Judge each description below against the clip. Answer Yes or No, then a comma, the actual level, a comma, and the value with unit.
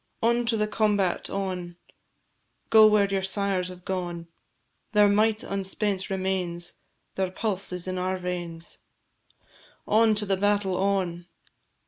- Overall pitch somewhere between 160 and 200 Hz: Yes, high, 190 Hz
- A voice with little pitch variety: Yes, narrow, 2.3 semitones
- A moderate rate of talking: No, slow, 130 wpm